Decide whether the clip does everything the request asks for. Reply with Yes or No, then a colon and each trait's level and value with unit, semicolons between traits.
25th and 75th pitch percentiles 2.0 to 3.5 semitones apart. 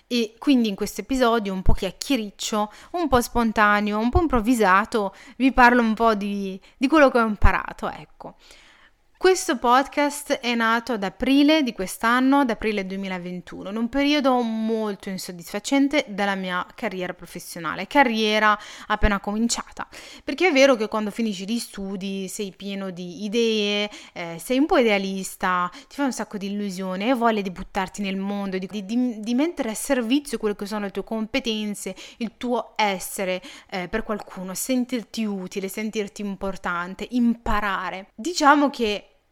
No: average, 4.1 semitones